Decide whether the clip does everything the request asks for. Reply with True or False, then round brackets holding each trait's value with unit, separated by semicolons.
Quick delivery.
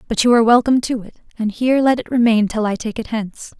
True (265 wpm)